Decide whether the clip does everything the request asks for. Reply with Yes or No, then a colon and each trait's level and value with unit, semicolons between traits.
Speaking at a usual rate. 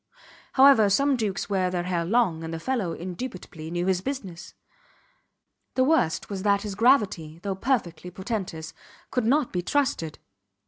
Yes: average, 150 wpm